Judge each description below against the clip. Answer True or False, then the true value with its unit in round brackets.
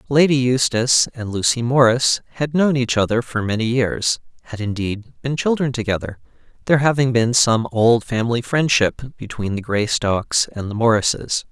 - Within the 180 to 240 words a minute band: False (145 wpm)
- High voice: False (120 Hz)